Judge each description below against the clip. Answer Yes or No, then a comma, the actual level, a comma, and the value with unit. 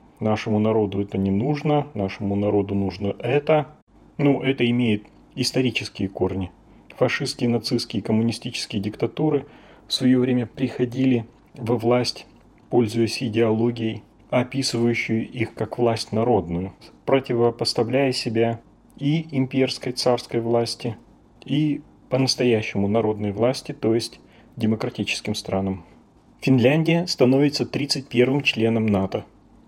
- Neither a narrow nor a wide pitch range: Yes, average, 3.2 semitones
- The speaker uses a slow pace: Yes, slow, 105 wpm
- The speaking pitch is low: Yes, low, 120 Hz